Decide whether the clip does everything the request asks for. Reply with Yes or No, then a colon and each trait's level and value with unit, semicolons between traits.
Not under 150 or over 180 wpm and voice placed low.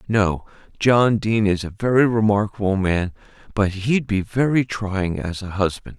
Yes: average, 160 wpm; low, 105 Hz